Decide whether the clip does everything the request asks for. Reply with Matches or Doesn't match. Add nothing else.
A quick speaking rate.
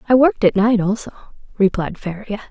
Doesn't match